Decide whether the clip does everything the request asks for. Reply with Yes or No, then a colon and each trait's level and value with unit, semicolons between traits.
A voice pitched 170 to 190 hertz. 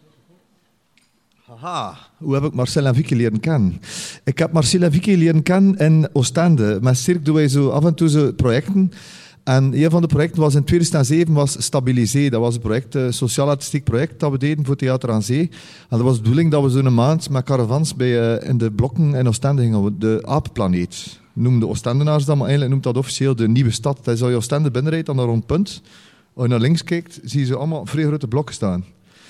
No: medium, 140 Hz